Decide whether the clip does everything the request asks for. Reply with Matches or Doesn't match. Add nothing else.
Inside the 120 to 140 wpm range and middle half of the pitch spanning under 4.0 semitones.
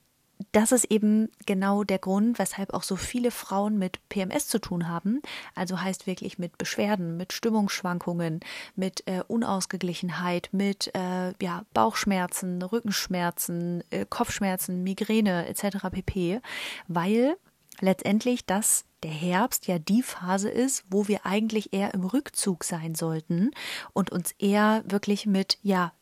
Matches